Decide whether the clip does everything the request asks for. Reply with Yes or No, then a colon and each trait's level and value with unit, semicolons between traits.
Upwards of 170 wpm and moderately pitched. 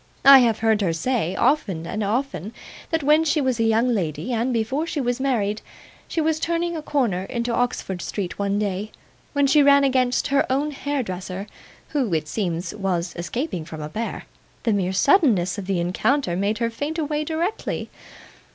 No: average, 180 wpm; high, 230 Hz